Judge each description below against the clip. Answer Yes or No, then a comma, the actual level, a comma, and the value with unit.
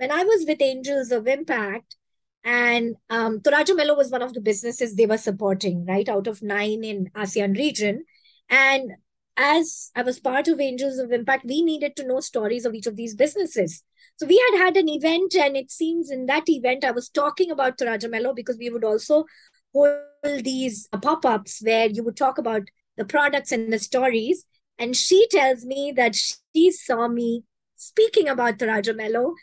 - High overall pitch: Yes, very high, 255 Hz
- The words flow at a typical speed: Yes, average, 180 wpm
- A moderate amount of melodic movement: Yes, average, 4.4 semitones